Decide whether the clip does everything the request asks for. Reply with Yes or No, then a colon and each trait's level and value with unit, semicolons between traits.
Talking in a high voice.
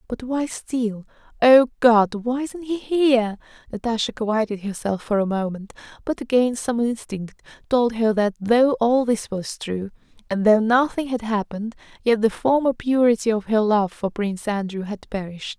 Yes: high, 225 Hz